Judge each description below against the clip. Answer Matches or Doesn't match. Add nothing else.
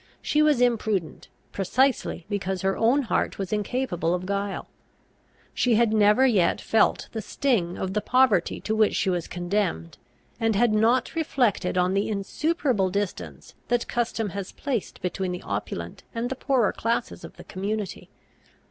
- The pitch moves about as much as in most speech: Matches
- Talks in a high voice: Matches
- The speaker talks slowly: Doesn't match